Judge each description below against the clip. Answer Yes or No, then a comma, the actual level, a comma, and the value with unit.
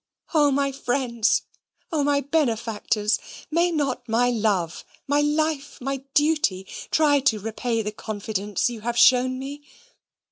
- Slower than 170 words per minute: Yes, slow, 135 wpm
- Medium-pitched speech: No, very high, 255 Hz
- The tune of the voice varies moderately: Yes, average, 4.5 semitones